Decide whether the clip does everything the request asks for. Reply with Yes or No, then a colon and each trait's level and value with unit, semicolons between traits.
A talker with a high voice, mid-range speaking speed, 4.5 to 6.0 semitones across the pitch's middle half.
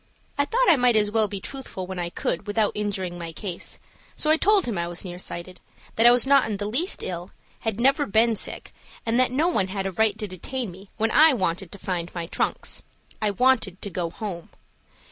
No: high, 210 Hz; fast, 225 wpm; average, 5.1 semitones